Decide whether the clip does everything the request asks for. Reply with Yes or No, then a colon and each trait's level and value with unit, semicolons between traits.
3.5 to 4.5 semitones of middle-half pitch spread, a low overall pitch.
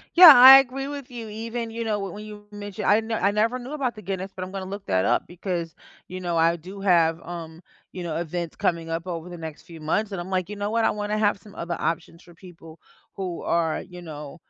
No: average, 4.0 semitones; high, 190 Hz